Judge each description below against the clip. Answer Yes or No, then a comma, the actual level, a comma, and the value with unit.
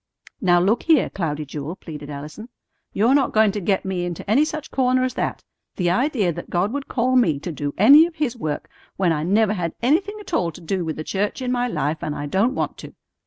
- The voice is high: Yes, high, 195 Hz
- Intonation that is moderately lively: No, wide, 7.6 semitones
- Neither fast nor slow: No, fast, 235 wpm